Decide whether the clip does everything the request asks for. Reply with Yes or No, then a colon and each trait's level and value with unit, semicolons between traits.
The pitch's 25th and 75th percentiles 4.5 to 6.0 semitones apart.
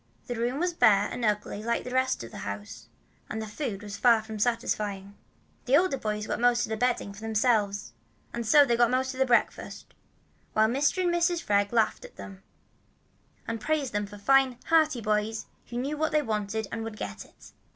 No: average, 3.8 semitones